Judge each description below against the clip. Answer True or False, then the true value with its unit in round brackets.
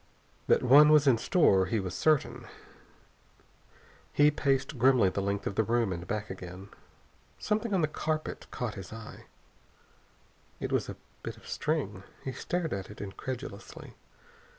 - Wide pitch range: True (7.1 semitones)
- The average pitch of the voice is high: False (120 Hz)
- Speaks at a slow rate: False (145 wpm)